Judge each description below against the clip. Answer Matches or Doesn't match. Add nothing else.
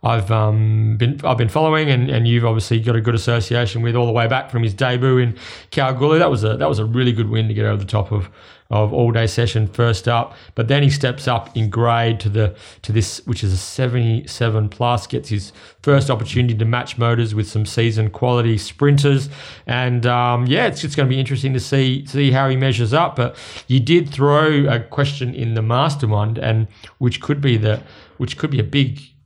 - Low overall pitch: Matches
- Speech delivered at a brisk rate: Matches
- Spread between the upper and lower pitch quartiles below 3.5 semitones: Matches